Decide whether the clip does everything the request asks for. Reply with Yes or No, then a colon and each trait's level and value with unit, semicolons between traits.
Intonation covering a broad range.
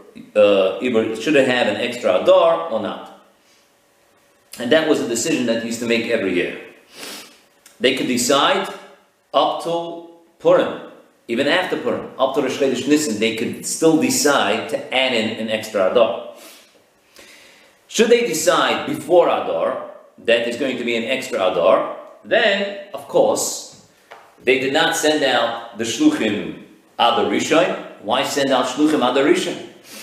Yes: wide, 5.9 semitones